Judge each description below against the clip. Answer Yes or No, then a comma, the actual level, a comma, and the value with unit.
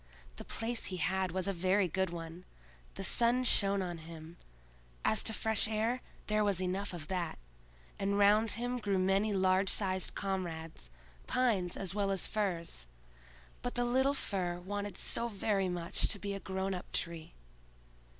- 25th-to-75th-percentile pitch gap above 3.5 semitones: No, average, 2.9 semitones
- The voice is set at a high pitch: Yes, high, 195 Hz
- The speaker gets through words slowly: No, average, 165 wpm